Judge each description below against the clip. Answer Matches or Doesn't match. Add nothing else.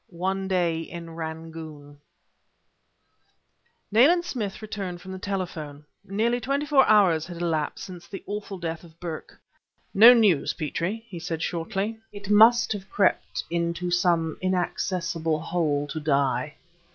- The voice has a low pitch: Doesn't match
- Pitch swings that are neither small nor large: Matches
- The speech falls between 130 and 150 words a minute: Matches